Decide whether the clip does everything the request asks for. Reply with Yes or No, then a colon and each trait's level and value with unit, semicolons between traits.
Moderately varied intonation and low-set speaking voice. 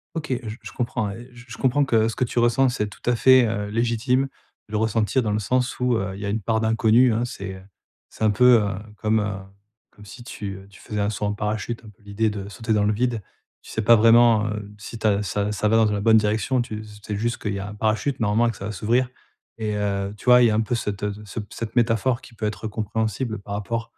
No: narrow, 2.3 semitones; low, 110 Hz